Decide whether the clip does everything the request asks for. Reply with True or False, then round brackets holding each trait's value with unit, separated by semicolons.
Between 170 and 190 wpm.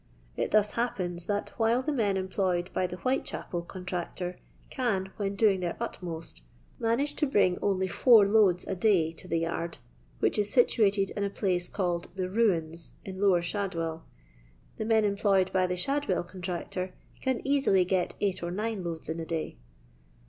True (175 wpm)